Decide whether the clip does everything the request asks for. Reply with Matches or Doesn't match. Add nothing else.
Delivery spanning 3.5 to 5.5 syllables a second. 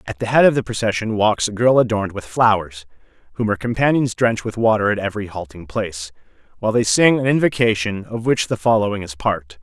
Doesn't match